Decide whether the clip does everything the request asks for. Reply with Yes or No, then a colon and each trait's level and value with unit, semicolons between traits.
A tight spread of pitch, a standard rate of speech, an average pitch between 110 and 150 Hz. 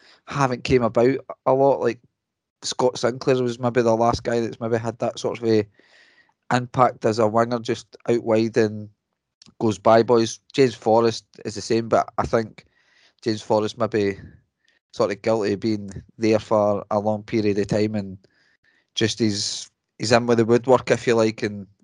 Yes: narrow, 2.1 semitones; average, 185 wpm; low, 115 Hz